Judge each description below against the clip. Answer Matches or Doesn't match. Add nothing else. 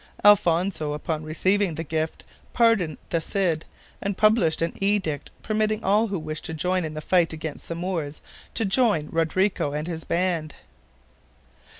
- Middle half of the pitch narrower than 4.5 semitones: Matches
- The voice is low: Doesn't match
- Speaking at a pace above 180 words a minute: Doesn't match